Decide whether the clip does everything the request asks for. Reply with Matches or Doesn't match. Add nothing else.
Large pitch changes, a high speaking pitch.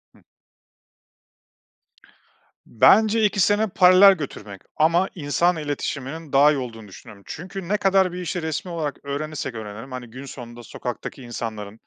Doesn't match